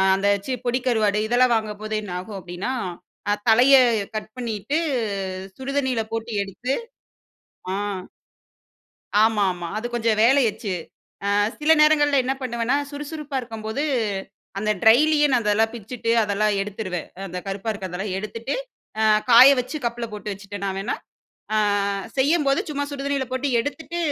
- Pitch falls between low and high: No, high, 230 Hz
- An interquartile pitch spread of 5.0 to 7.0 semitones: No, average, 4.2 semitones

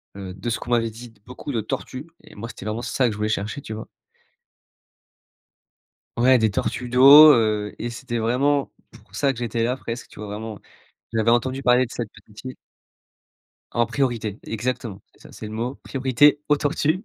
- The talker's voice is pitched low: Yes, low, 120 Hz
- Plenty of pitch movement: No, average, 2.9 semitones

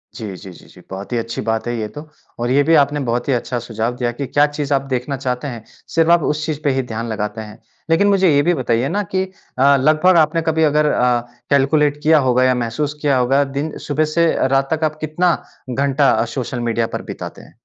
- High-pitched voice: No, medium, 140 Hz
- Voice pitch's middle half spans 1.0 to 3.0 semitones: No, average, 4.2 semitones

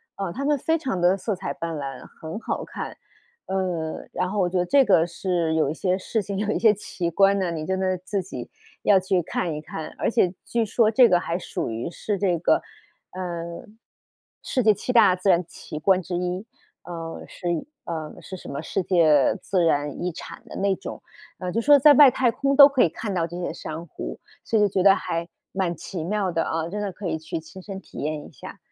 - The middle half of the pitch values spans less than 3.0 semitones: No, average, 3.4 semitones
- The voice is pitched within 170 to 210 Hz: Yes, medium, 185 Hz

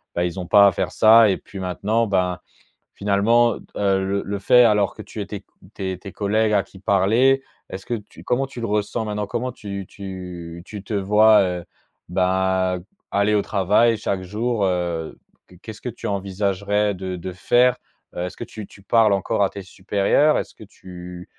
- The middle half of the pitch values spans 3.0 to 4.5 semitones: No, narrow, 2.5 semitones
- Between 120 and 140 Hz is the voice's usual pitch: No, low, 100 Hz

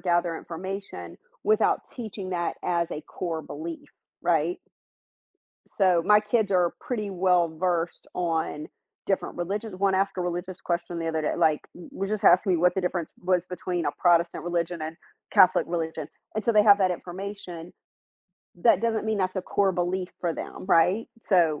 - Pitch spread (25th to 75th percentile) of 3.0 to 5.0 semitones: No, narrow, 2.4 semitones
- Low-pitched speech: No, medium, 180 Hz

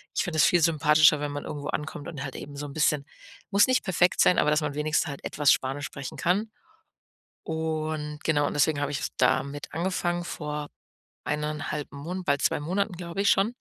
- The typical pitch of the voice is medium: Yes, medium, 150 Hz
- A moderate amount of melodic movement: Yes, average, 3.1 semitones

